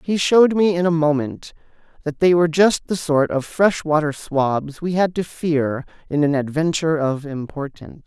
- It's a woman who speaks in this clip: No, male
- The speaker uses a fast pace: No, average, 185 wpm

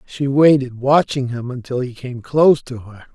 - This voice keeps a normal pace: Yes, average, 190 wpm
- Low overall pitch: Yes, low, 130 Hz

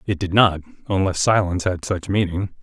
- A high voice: No, very low, 95 Hz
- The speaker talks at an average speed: Yes, average, 160 wpm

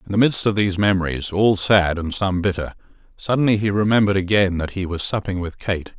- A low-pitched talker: Yes, very low, 95 Hz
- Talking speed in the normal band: No, fast, 210 wpm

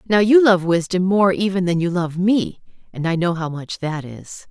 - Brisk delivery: Yes, fast, 225 wpm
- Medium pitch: Yes, medium, 180 Hz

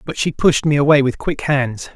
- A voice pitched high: No, medium, 140 Hz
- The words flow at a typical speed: No, fast, 245 wpm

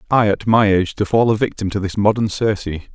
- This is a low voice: Yes, low, 105 Hz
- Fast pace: Yes, fast, 245 wpm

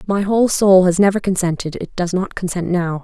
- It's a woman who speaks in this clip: Yes, female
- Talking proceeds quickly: Yes, fast, 220 wpm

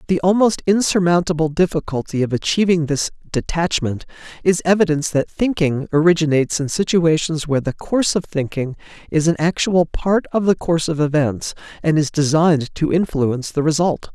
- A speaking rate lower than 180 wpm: Yes, average, 155 wpm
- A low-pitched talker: No, medium, 160 Hz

